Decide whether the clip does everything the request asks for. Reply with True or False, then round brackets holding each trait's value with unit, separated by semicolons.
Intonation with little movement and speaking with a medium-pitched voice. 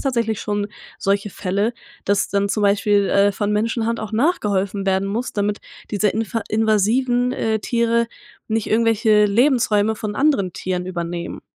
False (2.2 semitones; 210 Hz)